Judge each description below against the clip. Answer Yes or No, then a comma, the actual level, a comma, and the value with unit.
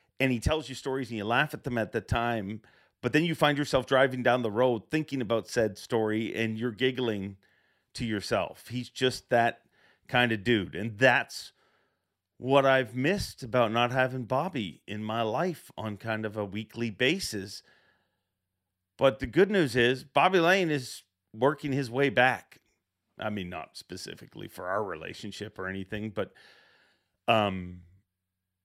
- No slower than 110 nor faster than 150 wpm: No, average, 165 wpm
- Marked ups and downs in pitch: No, average, 4.0 semitones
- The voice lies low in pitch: Yes, low, 115 Hz